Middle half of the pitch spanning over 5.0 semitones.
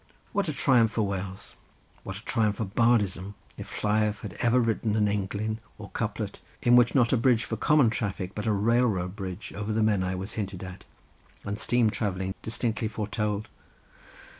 No: average, 2.7 semitones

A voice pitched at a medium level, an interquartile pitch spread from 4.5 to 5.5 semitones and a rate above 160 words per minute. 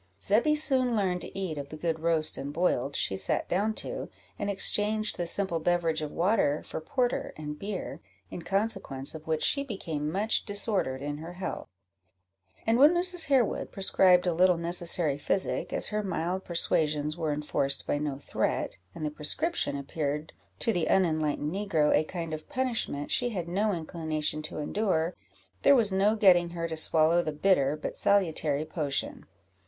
Yes: medium, 170 Hz; average, 4.8 semitones; average, 170 wpm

